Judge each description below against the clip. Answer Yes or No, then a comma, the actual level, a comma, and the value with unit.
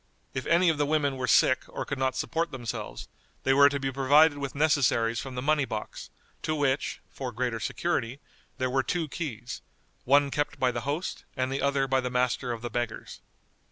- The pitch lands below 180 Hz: Yes, low, 135 Hz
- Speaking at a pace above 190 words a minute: Yes, average, 200 wpm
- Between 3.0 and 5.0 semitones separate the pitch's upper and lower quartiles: No, narrow, 2.5 semitones